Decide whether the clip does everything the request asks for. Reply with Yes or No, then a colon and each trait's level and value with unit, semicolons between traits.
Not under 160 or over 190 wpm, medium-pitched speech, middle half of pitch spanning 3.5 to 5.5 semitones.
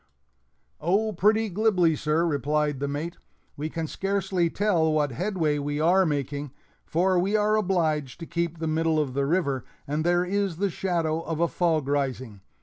Yes: average, 170 wpm; medium, 165 Hz; average, 3.9 semitones